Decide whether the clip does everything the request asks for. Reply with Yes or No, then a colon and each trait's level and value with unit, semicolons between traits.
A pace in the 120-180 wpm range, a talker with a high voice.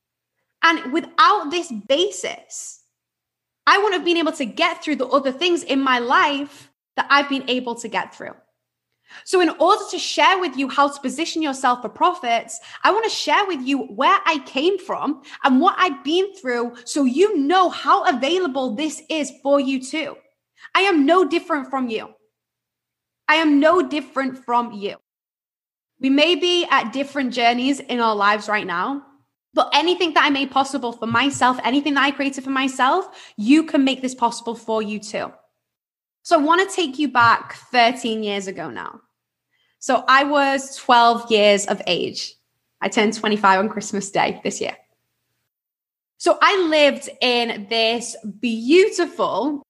Yes: average, 170 wpm; very high, 275 Hz